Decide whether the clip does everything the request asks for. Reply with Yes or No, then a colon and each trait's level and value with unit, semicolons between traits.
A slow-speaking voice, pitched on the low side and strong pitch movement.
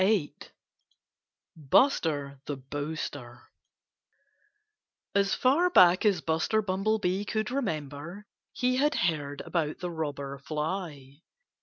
No: slow, 100 wpm; medium, 165 Hz; wide, 6.1 semitones